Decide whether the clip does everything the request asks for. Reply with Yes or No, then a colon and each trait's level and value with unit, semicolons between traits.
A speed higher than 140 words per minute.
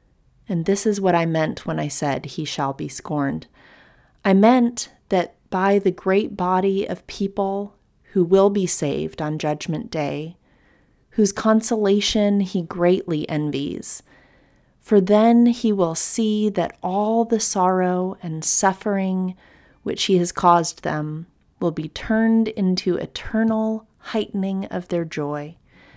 No: slow, 135 wpm